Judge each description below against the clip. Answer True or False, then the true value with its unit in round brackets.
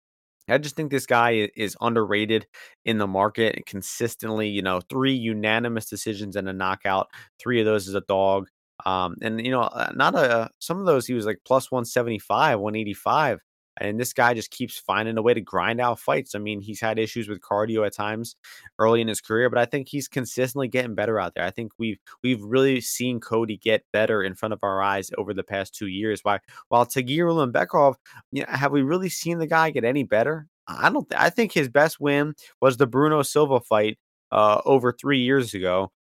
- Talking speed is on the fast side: True (215 wpm)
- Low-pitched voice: True (115 Hz)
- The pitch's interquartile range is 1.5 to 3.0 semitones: False (3.7 semitones)